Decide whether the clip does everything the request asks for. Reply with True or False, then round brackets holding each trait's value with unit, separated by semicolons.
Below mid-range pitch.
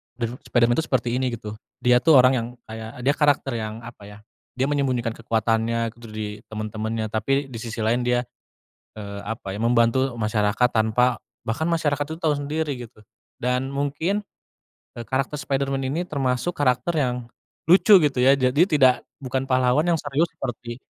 True (125 Hz)